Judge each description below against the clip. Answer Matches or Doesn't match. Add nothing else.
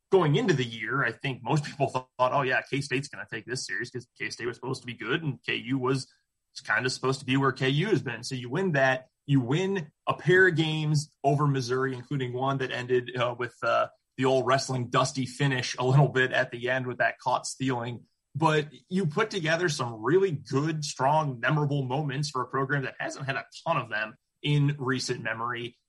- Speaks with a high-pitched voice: Doesn't match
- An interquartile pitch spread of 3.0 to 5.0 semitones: Doesn't match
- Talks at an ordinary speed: Doesn't match